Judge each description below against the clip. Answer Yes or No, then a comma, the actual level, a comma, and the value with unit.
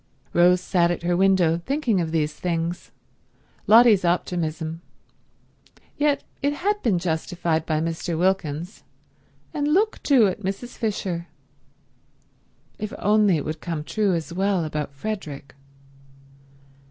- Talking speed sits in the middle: No, slow, 125 wpm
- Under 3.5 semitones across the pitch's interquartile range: No, average, 4.5 semitones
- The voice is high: No, medium, 180 Hz